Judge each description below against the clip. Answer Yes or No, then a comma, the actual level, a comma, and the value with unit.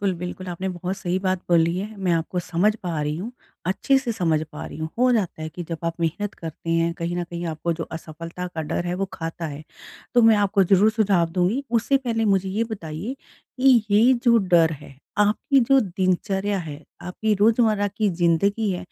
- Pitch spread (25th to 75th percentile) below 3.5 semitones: No, average, 4.0 semitones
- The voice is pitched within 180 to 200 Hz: Yes, medium, 185 Hz